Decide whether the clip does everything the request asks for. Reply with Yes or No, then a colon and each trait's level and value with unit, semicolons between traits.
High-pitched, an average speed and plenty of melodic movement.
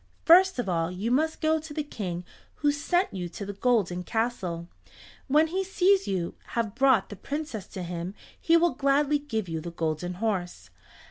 Yes: high, 225 Hz; average, 185 wpm; wide, 8.9 semitones